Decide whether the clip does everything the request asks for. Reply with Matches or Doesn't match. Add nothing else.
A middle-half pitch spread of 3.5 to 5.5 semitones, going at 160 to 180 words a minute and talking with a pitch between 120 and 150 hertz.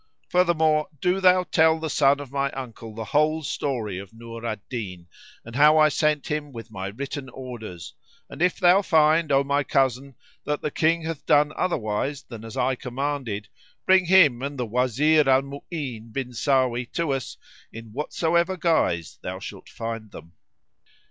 Matches